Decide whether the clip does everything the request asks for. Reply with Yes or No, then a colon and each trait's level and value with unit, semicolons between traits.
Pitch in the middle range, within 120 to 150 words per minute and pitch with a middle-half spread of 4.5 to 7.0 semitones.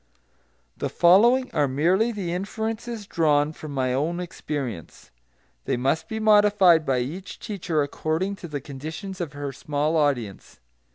Yes: medium, 160 Hz; average, 140 wpm; wide, 5.4 semitones